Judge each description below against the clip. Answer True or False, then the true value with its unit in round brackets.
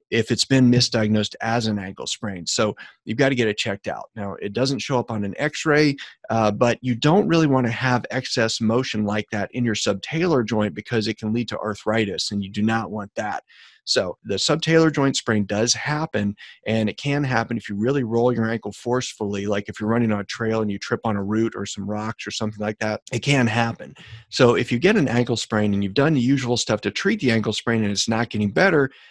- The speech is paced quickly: True (240 wpm)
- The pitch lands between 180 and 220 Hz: False (115 Hz)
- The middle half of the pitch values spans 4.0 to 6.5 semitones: False (2.8 semitones)